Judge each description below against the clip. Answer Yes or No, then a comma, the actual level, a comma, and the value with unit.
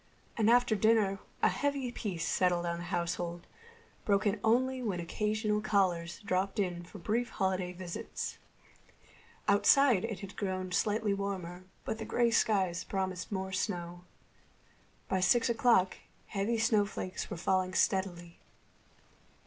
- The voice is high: Yes, high, 195 Hz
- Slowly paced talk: Yes, slow, 130 wpm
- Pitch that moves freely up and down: No, average, 3.3 semitones